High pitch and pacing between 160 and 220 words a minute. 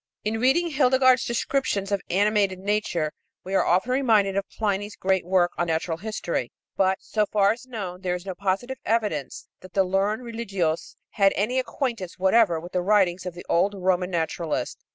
Yes: high, 195 Hz; average, 175 wpm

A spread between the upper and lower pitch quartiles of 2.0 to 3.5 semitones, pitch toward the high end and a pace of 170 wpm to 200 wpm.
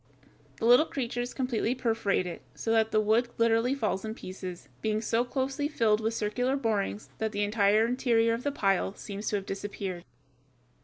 Yes: average, 2.9 semitones; high, 225 Hz; average, 175 wpm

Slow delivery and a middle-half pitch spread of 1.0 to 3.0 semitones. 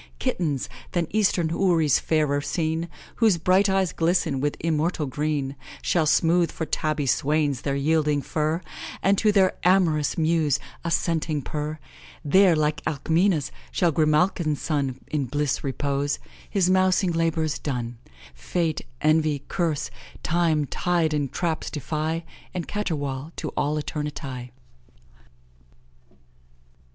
Yes: slow, 120 wpm; average, 2.7 semitones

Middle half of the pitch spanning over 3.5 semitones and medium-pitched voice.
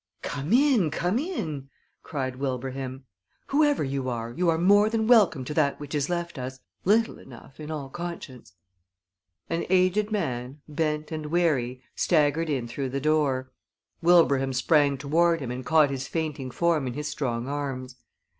Yes: average, 4.4 semitones; medium, 150 Hz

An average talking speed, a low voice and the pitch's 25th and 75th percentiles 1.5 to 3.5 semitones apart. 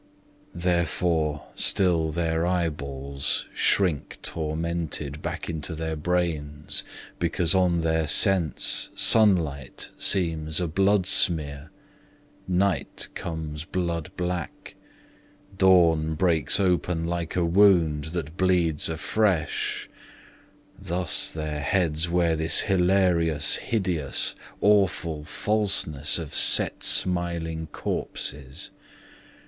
No: slow, 90 wpm; very low, 85 Hz; average, 2.7 semitones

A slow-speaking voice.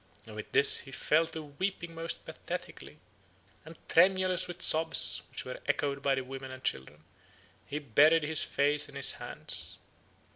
No: average, 160 wpm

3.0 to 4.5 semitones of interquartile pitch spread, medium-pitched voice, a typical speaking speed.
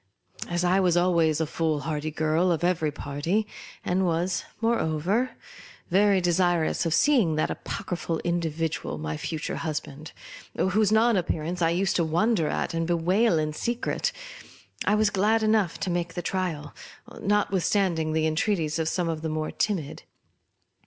Yes: average, 3.5 semitones; medium, 175 Hz; average, 150 wpm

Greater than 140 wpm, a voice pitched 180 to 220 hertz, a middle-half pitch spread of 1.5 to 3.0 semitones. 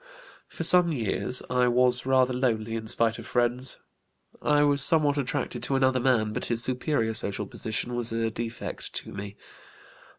No: average, 165 wpm; low, 125 Hz; average, 2.7 semitones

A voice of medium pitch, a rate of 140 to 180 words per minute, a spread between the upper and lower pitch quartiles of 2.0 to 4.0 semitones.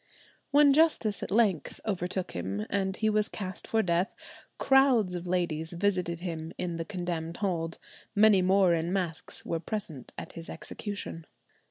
Yes: medium, 180 Hz; average, 155 wpm; average, 3.7 semitones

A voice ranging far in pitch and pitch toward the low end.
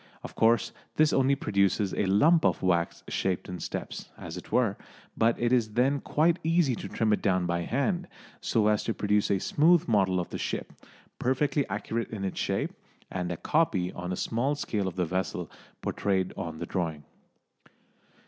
Yes: wide, 6.0 semitones; low, 105 Hz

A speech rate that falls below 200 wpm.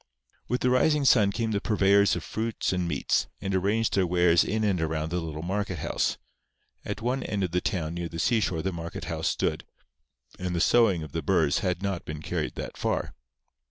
No: fast, 205 wpm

